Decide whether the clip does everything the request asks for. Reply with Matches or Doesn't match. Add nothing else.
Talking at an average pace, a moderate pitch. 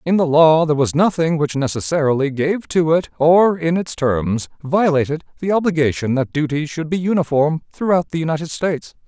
Matches